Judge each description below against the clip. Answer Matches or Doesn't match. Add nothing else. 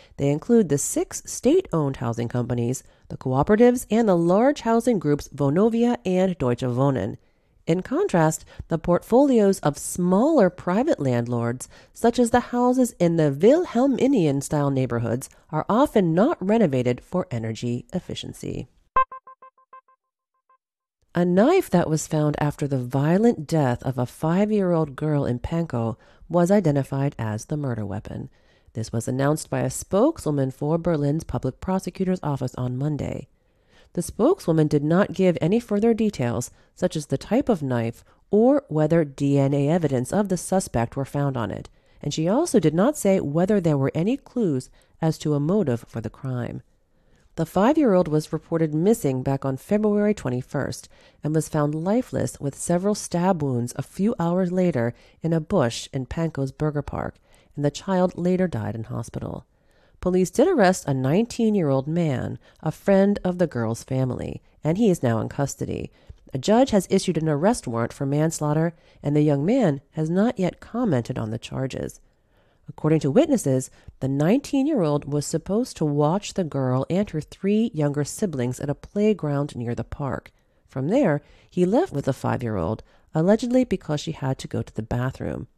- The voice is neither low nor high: Matches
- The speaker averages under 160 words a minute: Doesn't match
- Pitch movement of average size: Doesn't match